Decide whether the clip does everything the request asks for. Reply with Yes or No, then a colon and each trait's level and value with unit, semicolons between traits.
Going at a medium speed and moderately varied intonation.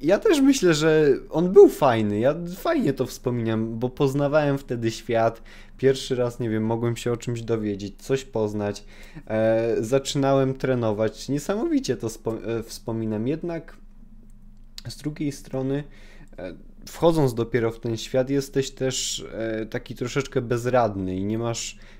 Yes: average, 145 wpm; average, 3.8 semitones